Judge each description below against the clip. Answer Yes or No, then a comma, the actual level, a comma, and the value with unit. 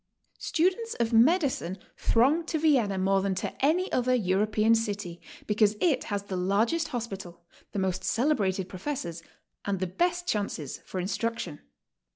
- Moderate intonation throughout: No, wide, 6.7 semitones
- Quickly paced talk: No, average, 150 wpm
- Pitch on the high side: Yes, high, 215 Hz